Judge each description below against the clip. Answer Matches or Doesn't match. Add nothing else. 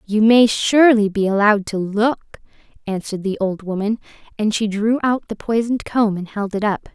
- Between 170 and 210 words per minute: Matches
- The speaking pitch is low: Doesn't match